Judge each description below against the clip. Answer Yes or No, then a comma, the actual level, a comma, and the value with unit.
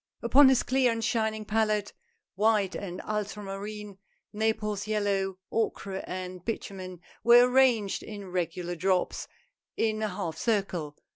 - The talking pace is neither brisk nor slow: No, slow, 125 wpm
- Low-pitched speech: No, high, 210 Hz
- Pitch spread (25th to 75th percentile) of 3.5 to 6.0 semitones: No, average, 2.7 semitones